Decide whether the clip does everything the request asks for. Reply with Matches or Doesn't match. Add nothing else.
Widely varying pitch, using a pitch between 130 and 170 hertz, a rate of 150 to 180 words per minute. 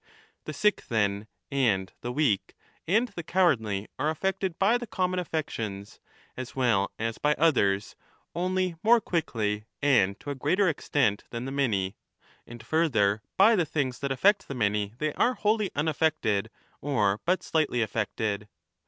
Matches